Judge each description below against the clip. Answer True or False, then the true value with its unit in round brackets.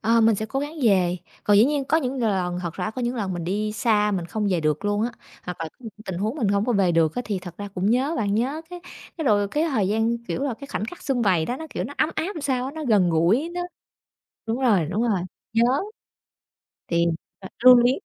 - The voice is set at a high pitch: True (215 Hz)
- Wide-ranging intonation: False (4.9 semitones)